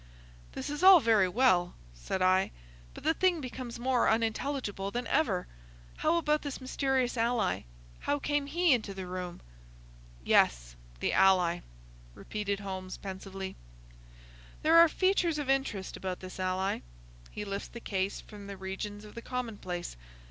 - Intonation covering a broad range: Yes, wide, 6.1 semitones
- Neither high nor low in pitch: No, high, 210 Hz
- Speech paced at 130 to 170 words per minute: Yes, average, 150 wpm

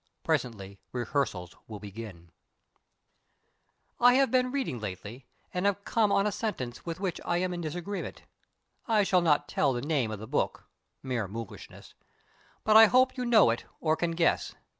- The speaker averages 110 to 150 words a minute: No, average, 170 wpm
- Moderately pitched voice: Yes, medium, 160 Hz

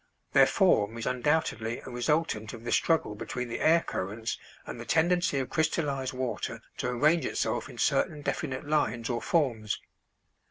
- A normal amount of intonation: Yes, average, 5.0 semitones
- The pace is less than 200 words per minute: Yes, average, 160 wpm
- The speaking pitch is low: Yes, low, 130 Hz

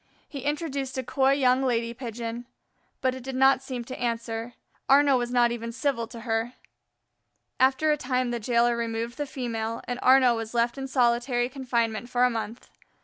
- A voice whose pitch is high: Yes, high, 245 Hz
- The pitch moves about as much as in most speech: No, narrow, 2.1 semitones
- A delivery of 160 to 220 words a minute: Yes, average, 180 wpm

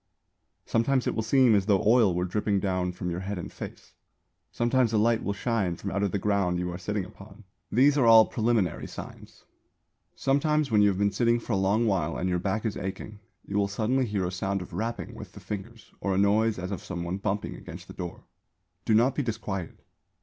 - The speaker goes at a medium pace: No, fast, 225 wpm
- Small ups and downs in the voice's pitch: No, average, 3.3 semitones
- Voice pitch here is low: Yes, low, 105 Hz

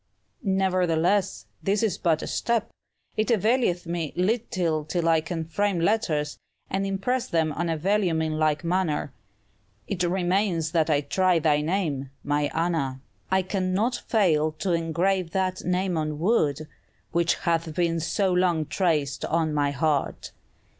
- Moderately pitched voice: Yes, medium, 170 Hz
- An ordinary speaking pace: Yes, average, 145 wpm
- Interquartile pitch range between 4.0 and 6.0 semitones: No, average, 3.4 semitones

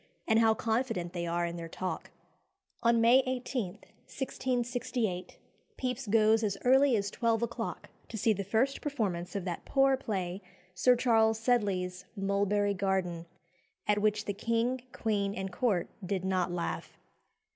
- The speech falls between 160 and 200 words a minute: No, average, 145 wpm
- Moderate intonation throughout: Yes, average, 4.0 semitones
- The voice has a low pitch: No, high, 215 Hz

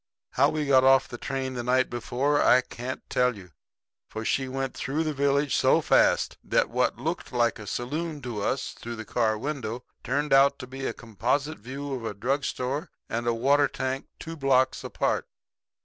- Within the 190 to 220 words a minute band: Yes, average, 195 wpm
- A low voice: Yes, low, 130 Hz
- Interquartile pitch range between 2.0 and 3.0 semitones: Yes, narrow, 2.6 semitones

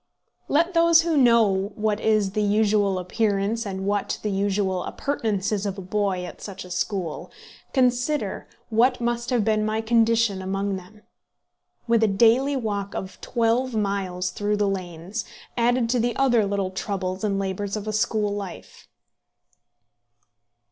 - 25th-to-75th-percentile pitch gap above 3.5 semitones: No, average, 3.0 semitones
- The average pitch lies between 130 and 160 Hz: No, high, 210 Hz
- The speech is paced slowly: No, average, 150 wpm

